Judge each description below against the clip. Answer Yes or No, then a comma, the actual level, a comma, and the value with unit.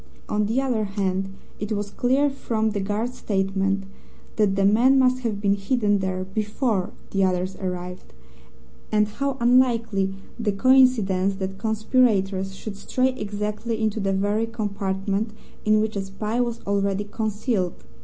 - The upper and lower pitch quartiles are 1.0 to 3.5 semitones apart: Yes, average, 2.8 semitones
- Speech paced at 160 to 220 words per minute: No, average, 145 wpm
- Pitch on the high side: Yes, high, 210 Hz